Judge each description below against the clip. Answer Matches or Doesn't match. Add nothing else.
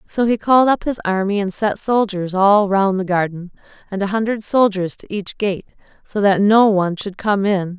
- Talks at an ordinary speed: Doesn't match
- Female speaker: Matches